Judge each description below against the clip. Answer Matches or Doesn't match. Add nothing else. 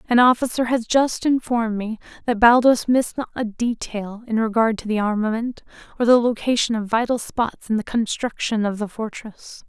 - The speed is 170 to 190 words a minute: Matches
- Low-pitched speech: Doesn't match